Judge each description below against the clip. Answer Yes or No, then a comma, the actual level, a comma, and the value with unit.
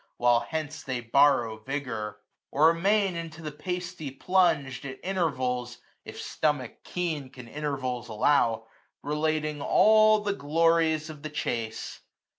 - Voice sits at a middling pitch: Yes, medium, 150 Hz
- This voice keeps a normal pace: No, slow, 130 wpm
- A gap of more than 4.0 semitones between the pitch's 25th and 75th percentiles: Yes, average, 4.8 semitones